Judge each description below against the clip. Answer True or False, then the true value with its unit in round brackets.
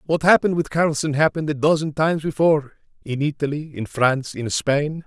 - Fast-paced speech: False (165 wpm)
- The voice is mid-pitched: True (150 Hz)